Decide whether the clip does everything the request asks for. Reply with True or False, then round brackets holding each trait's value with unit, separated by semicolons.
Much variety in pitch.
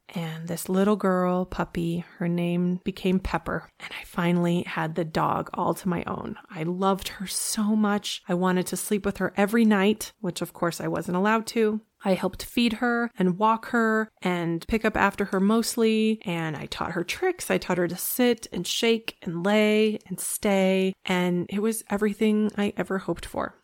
False (3.3 semitones)